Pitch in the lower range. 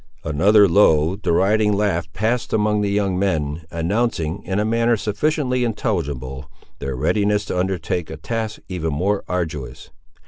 Yes: very low, 95 Hz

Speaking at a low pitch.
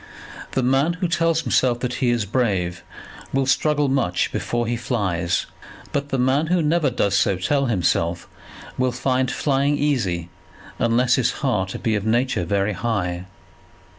Yes: low, 125 Hz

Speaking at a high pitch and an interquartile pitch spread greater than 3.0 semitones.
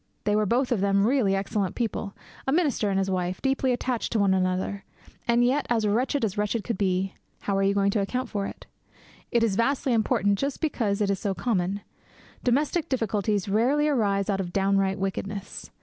Yes: high, 205 Hz; average, 3.7 semitones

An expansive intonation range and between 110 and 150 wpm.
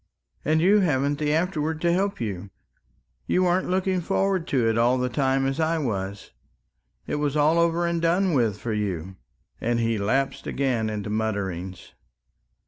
No: wide, 7.4 semitones; average, 170 wpm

